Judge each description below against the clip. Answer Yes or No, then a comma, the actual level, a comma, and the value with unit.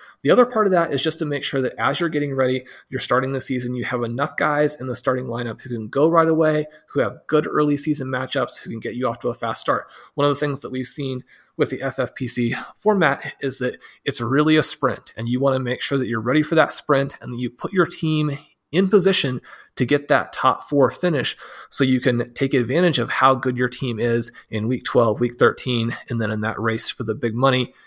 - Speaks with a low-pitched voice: Yes, low, 130 Hz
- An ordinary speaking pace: No, fast, 250 wpm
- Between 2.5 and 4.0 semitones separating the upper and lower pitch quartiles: Yes, average, 3.3 semitones